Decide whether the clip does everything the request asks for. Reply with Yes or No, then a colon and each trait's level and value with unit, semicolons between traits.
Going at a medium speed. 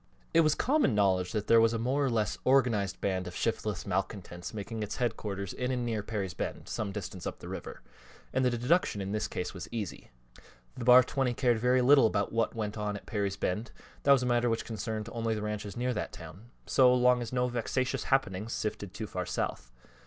No: fast, 215 wpm